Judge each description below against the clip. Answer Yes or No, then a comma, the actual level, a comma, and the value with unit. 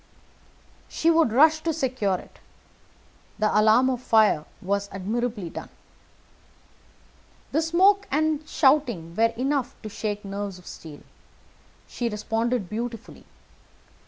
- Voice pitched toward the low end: No, high, 230 Hz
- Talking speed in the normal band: No, slow, 115 wpm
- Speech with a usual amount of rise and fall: No, wide, 5.8 semitones